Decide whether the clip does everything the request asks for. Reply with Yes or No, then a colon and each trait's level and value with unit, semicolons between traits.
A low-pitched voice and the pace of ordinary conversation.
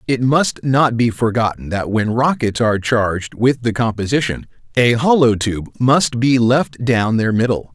Yes: low, 120 Hz; average, 170 wpm